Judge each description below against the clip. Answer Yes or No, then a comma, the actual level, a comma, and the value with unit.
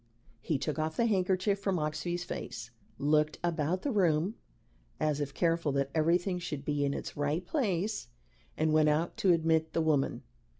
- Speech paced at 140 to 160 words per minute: No, average, 170 wpm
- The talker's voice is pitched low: No, medium, 160 Hz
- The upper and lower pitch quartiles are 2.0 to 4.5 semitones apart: Yes, average, 3.0 semitones